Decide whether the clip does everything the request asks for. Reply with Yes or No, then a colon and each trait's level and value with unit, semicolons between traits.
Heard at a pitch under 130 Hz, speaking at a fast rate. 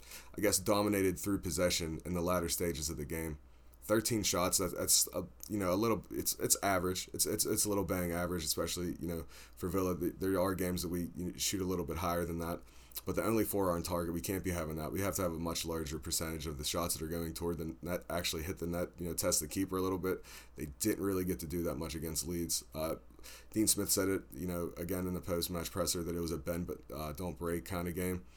Yes: very low, 85 Hz; fast, 255 wpm